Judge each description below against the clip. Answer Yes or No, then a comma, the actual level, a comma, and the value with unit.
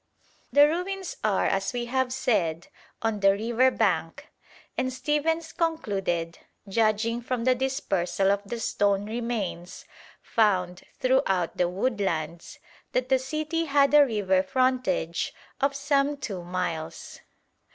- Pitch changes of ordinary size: No, wide, 5.7 semitones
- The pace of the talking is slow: Yes, slow, 125 wpm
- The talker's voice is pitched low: No, high, 230 Hz